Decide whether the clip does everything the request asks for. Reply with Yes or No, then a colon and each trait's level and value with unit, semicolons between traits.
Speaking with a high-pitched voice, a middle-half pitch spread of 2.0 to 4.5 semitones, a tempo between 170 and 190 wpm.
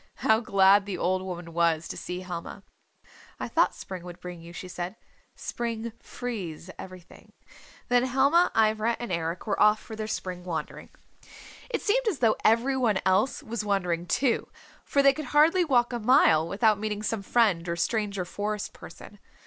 No: high, 210 Hz; average, 5.0 semitones; average, 175 wpm